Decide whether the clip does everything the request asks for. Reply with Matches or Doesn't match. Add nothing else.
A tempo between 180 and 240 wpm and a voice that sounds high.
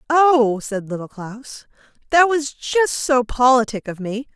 Doesn't match